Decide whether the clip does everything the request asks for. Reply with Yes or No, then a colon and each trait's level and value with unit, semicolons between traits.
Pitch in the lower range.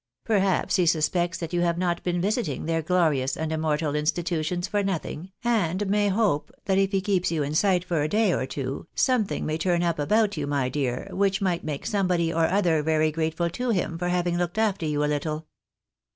No: medium, 170 Hz